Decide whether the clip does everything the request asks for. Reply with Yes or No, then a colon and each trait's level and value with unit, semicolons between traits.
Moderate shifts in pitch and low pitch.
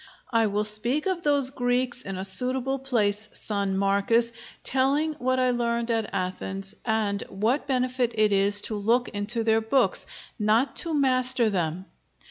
No: average, 3.9 semitones; high, 230 Hz